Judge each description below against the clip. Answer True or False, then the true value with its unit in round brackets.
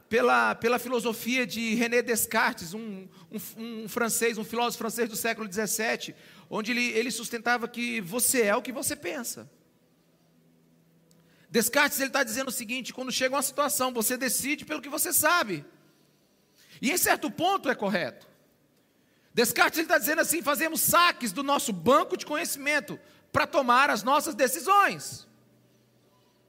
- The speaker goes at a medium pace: True (150 wpm)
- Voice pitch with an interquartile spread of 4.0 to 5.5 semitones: True (4.3 semitones)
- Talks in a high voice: True (245 Hz)